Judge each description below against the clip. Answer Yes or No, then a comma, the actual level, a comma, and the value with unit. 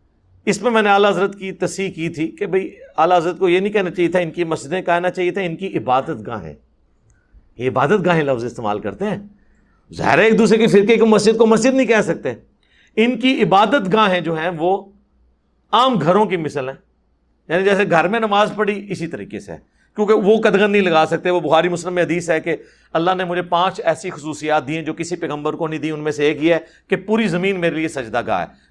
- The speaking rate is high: Yes, fast, 235 wpm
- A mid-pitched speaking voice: Yes, medium, 180 Hz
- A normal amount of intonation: Yes, average, 4.3 semitones